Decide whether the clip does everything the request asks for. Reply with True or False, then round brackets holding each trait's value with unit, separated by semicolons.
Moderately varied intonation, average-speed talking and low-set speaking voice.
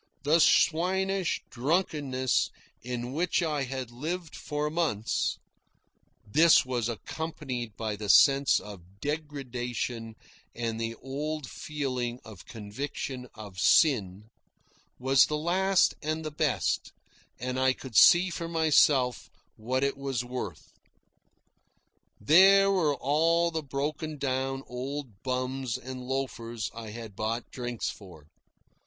False (4.4 semitones; 115 wpm; 130 Hz)